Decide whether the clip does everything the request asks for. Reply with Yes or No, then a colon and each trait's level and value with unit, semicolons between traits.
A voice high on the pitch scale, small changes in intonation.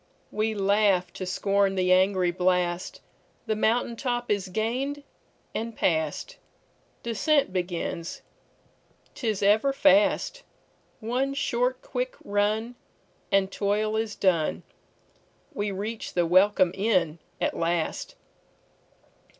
No: high, 205 Hz; average, 4.2 semitones